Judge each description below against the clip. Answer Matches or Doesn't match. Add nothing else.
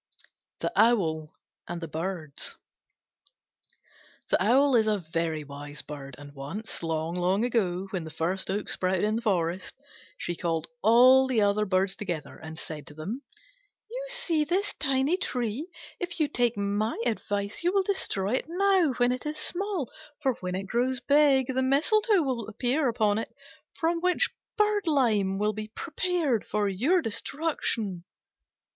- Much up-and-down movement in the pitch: Matches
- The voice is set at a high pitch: Matches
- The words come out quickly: Doesn't match